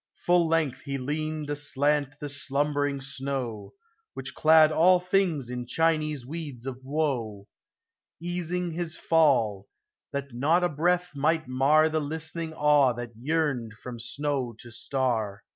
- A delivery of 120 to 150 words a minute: Yes, average, 140 wpm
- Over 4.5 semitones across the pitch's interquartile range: No, average, 3.7 semitones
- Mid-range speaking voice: Yes, medium, 145 Hz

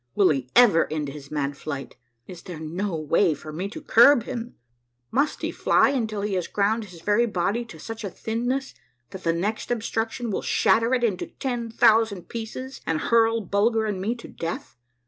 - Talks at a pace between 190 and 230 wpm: Yes, average, 195 wpm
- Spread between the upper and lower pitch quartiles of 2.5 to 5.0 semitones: No, wide, 5.4 semitones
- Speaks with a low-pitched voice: No, high, 210 Hz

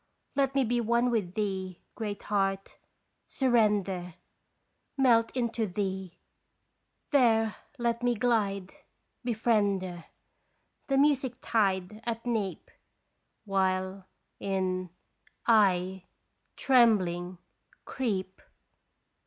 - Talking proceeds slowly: Yes, slow, 85 wpm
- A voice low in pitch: No, high, 210 Hz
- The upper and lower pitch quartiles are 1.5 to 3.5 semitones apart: No, average, 3.9 semitones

